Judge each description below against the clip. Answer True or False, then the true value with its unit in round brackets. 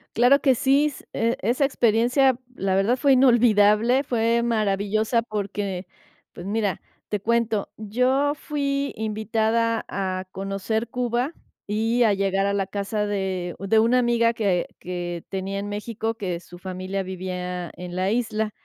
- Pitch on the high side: True (215 Hz)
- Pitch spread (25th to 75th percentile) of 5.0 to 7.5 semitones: False (3.4 semitones)